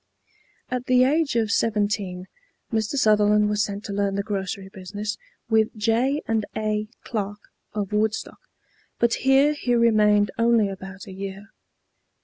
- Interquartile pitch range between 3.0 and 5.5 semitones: No, narrow, 2.4 semitones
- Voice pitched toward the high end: Yes, high, 210 Hz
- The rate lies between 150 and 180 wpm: No, average, 140 wpm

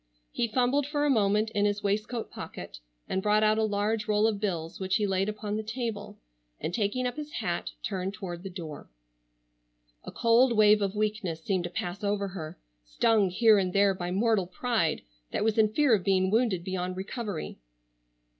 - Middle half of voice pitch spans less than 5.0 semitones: Yes, average, 2.9 semitones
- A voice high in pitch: Yes, high, 205 Hz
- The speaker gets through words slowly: No, average, 190 wpm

